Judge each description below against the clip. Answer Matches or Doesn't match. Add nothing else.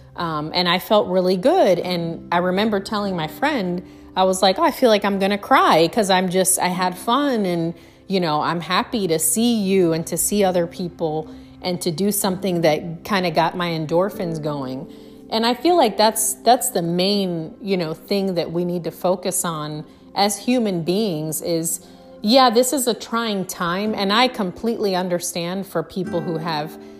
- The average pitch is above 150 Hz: Matches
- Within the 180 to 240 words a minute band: Matches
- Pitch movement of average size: Matches